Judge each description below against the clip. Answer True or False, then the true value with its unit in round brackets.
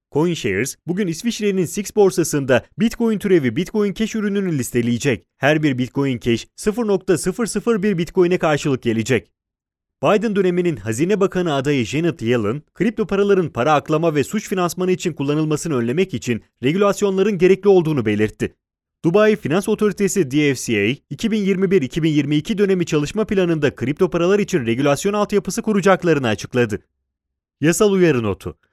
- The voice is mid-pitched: True (170 Hz)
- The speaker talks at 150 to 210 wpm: False (125 wpm)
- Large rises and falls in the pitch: True (7.1 semitones)